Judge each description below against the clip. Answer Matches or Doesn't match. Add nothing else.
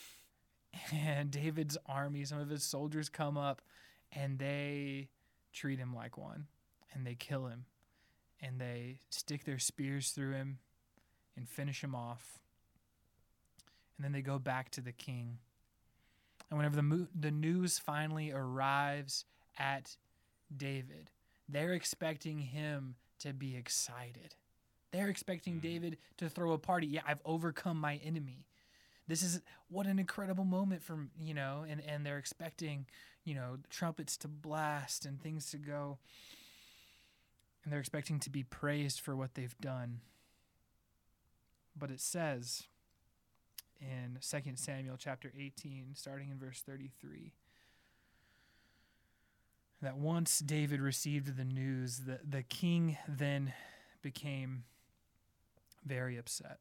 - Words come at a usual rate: Doesn't match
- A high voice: Doesn't match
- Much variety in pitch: Doesn't match